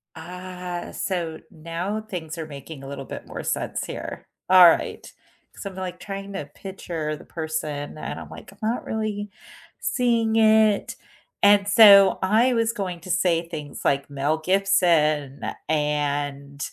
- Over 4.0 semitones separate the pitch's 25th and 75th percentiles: Yes, average, 4.7 semitones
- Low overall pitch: No, medium, 175 Hz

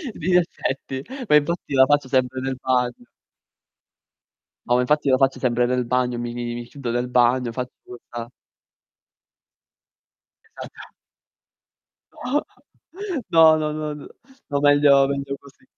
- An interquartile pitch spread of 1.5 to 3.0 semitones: Yes, average, 2.7 semitones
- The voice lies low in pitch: Yes, low, 130 Hz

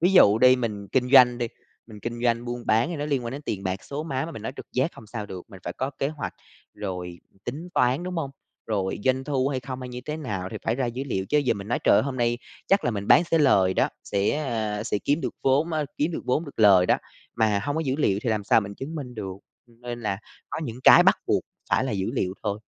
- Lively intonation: No, average, 4.9 semitones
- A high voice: No, low, 120 Hz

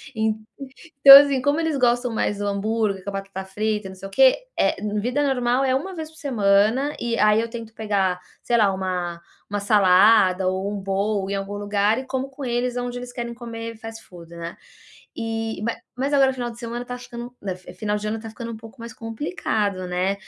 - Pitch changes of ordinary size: Yes, average, 3.6 semitones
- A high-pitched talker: Yes, high, 225 Hz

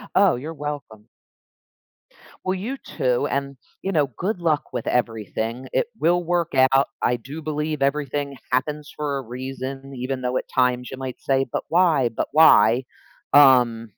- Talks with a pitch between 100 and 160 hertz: Yes, medium, 140 Hz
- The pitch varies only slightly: No, average, 3.4 semitones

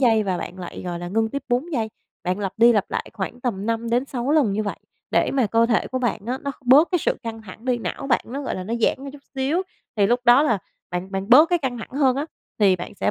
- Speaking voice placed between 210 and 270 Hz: Yes, high, 235 Hz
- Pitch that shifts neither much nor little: Yes, average, 4.6 semitones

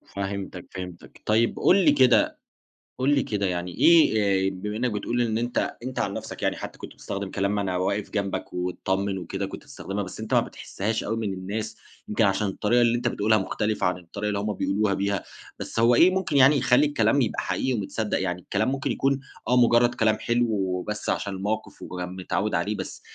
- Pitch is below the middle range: Yes, low, 105 Hz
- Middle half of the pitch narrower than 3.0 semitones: No, average, 3.6 semitones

